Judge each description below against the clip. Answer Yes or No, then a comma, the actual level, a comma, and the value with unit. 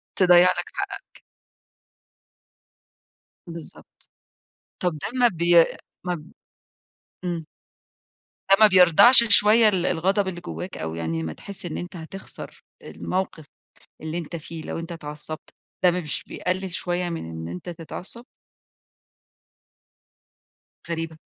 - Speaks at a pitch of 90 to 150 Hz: No, medium, 175 Hz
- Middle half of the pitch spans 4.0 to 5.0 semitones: No, average, 2.8 semitones